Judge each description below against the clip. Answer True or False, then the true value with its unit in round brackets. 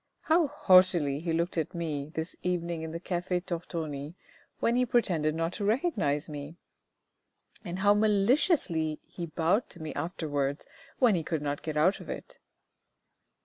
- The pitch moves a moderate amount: True (4.0 semitones)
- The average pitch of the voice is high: False (170 Hz)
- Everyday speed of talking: True (155 wpm)